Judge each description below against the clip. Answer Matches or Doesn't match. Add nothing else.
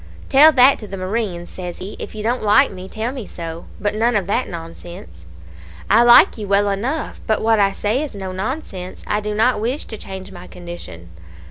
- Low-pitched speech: Doesn't match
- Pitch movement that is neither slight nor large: Matches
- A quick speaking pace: Matches